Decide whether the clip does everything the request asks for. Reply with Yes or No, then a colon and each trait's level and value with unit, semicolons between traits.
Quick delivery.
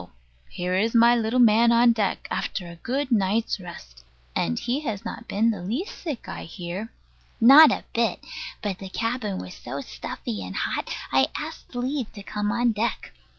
No: average, 180 wpm